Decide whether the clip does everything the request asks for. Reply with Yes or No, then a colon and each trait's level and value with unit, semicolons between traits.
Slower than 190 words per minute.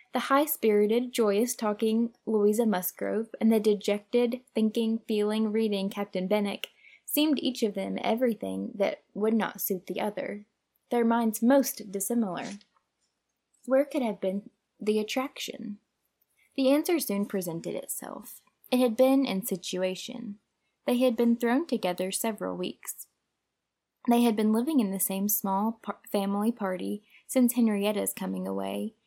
Yes: average, 140 wpm